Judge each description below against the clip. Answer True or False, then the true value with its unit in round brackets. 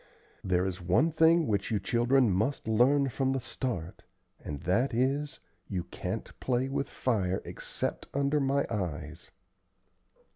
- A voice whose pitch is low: True (120 Hz)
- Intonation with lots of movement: True (6.7 semitones)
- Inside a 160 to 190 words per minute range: False (140 wpm)